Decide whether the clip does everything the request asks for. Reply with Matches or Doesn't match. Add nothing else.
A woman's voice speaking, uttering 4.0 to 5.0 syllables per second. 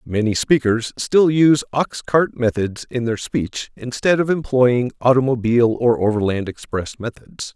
Doesn't match